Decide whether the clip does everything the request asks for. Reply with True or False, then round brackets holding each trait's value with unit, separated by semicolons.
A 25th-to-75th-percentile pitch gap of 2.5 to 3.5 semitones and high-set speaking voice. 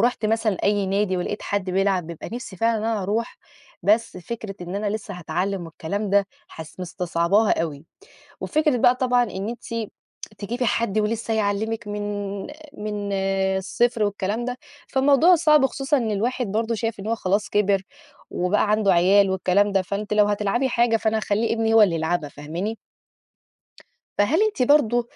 True (3.0 semitones; 210 Hz)